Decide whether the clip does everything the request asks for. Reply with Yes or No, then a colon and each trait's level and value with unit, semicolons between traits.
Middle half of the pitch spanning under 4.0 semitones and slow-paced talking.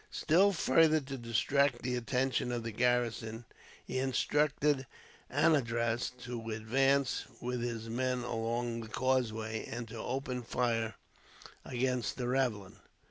Yes: narrow, 2.4 semitones; slow, 125 wpm